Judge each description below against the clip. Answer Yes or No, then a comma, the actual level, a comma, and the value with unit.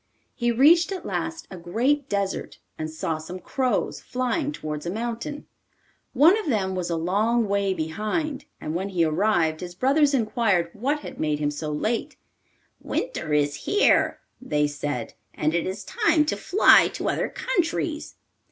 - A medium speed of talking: Yes, average, 160 wpm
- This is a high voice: Yes, high, 205 Hz